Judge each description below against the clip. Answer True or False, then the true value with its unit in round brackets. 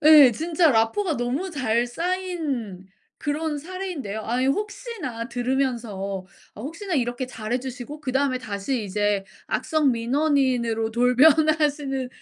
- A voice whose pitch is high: True (265 Hz)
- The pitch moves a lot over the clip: False (4.9 semitones)